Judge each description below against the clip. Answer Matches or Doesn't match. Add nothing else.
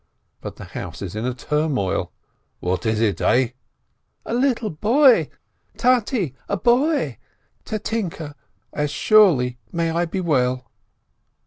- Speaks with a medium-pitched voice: Matches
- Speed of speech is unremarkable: Doesn't match